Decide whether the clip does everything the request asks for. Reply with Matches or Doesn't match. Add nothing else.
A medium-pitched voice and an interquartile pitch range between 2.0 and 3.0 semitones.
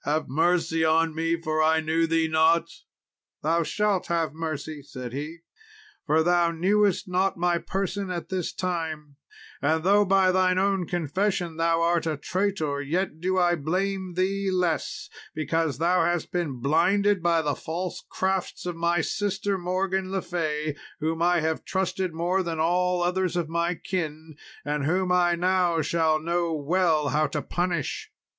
Matches